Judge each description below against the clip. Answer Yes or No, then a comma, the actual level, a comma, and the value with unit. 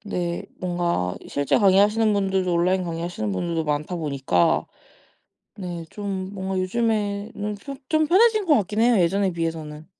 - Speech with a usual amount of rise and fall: Yes, average, 3.7 semitones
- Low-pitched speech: No, medium, 185 Hz